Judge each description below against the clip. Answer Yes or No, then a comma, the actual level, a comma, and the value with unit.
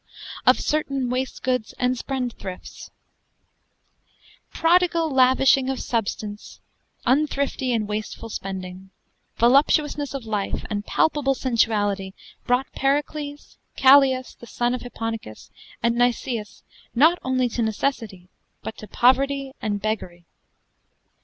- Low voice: No, very high, 250 Hz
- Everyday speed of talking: No, slow, 105 wpm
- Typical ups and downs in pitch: Yes, average, 4.0 semitones